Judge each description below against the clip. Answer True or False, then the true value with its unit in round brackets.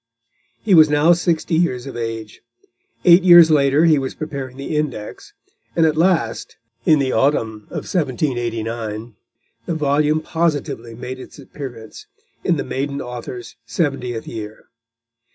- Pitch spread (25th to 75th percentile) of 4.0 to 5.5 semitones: True (4.9 semitones)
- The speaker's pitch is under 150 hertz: True (140 Hz)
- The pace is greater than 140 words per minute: False (135 wpm)